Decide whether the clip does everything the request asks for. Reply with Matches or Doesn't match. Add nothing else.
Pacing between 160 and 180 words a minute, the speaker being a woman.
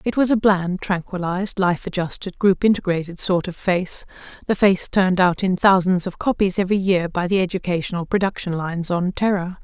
Matches